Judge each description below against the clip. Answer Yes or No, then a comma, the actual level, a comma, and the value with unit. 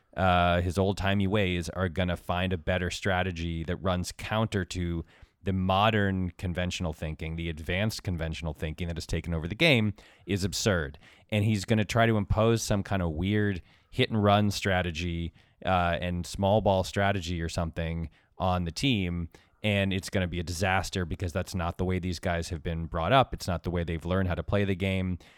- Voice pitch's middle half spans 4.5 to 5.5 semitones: No, narrow, 2.5 semitones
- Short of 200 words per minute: No, fast, 205 wpm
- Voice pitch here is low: Yes, very low, 90 Hz